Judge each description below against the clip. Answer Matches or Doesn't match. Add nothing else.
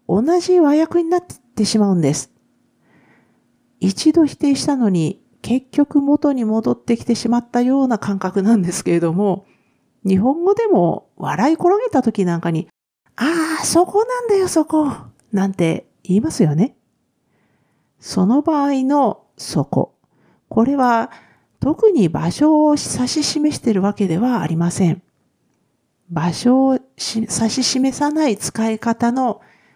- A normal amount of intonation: Doesn't match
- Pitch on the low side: Doesn't match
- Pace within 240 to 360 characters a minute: Matches